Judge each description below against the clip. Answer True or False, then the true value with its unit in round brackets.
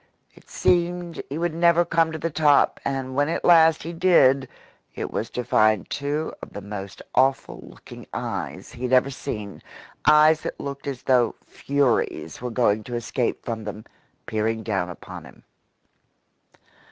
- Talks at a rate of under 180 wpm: True (165 wpm)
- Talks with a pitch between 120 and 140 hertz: True (135 Hz)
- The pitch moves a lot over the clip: True (6.0 semitones)